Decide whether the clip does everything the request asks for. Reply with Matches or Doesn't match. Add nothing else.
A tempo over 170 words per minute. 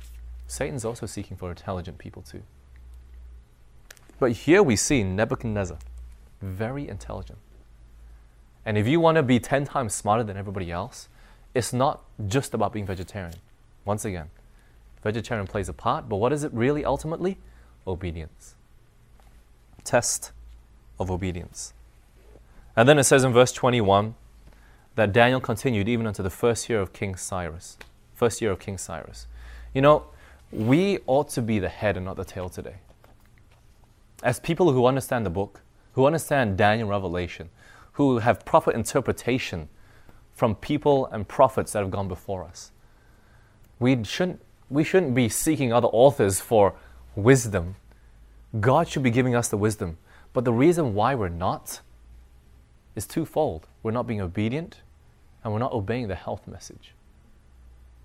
Doesn't match